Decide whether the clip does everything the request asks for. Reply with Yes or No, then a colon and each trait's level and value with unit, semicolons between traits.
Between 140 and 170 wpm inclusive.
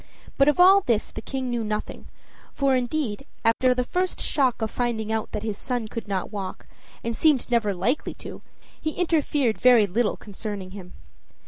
No: average, 180 wpm